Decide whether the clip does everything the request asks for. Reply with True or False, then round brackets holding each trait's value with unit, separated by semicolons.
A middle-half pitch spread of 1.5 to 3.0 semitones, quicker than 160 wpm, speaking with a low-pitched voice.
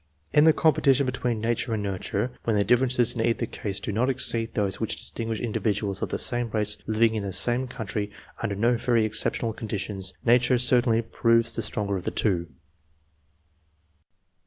True (2.7 semitones; 180 wpm; 115 Hz)